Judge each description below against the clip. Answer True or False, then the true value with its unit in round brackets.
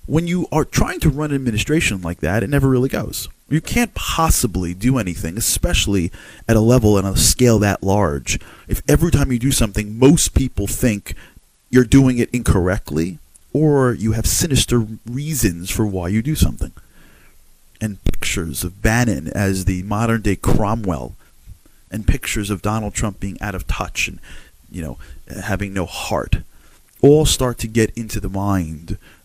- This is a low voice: True (105 Hz)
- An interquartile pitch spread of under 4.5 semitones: False (5.3 semitones)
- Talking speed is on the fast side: False (170 wpm)